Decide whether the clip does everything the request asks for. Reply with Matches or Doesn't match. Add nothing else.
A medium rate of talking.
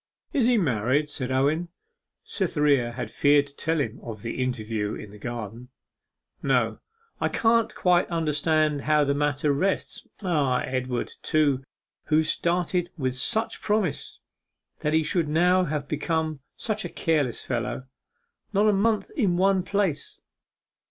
Matches